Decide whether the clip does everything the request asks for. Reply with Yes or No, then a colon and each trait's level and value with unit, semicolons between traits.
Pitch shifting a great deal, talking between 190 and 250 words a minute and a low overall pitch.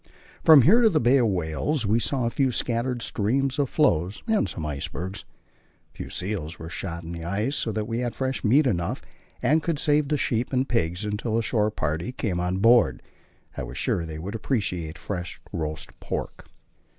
Yes: wide, 6.9 semitones; average, 200 wpm; low, 110 Hz